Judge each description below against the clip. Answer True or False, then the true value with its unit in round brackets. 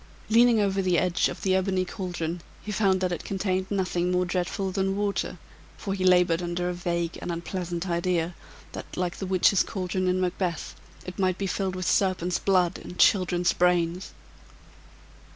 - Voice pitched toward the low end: False (185 Hz)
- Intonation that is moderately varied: False (1.5 semitones)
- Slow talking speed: False (170 wpm)